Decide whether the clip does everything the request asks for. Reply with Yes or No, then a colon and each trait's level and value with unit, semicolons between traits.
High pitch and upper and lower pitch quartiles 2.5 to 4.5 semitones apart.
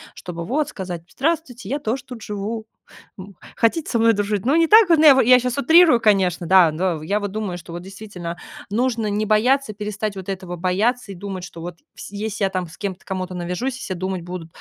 No: high, 205 Hz; average, 4.9 semitones